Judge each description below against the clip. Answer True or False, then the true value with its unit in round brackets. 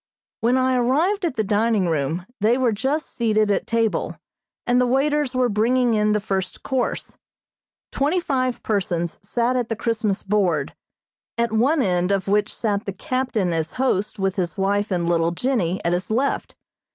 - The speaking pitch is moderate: False (220 Hz)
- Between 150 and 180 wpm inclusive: True (175 wpm)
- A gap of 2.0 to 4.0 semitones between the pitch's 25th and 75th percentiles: False (4.8 semitones)